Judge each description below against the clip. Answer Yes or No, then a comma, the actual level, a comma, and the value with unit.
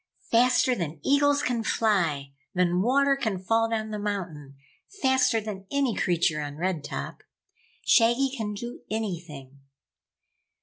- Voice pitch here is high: Yes, high, 210 Hz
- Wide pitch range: Yes, wide, 6.0 semitones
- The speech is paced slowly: Yes, slow, 130 wpm